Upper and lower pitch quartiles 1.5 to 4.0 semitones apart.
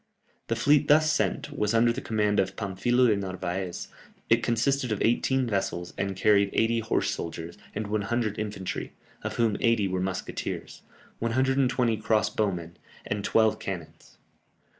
Yes: average, 3.4 semitones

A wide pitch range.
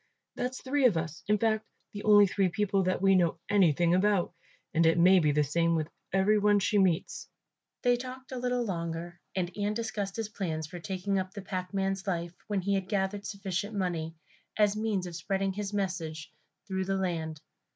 No: average, 3.2 semitones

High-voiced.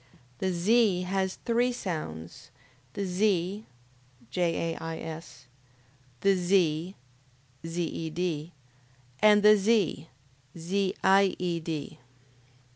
No: medium, 180 Hz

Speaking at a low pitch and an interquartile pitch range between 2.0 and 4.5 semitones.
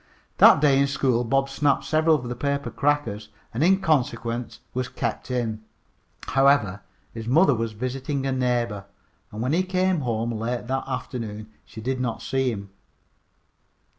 Yes: low, 125 Hz; average, 3.4 semitones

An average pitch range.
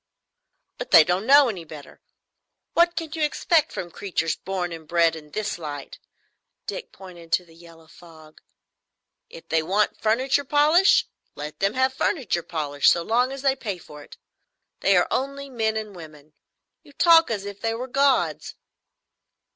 No: wide, 8.5 semitones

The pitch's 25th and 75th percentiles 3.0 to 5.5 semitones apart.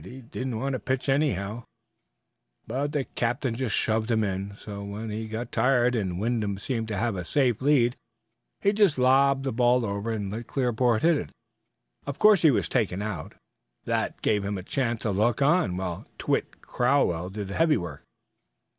Yes: average, 4.6 semitones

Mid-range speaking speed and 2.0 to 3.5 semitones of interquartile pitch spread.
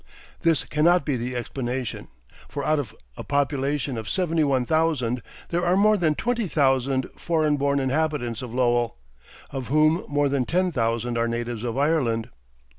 No: average, 165 wpm; average, 4.4 semitones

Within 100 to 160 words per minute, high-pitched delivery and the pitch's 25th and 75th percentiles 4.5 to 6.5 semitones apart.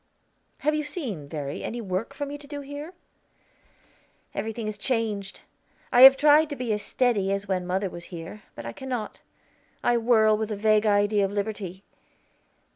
No: average, 175 wpm; high, 215 Hz; average, 5.0 semitones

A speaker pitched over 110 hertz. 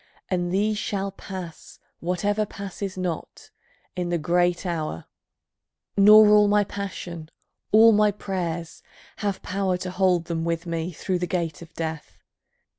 Yes: medium, 185 Hz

